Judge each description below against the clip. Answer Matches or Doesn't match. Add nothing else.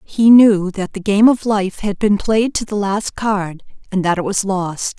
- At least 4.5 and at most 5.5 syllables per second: Doesn't match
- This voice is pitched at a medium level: Doesn't match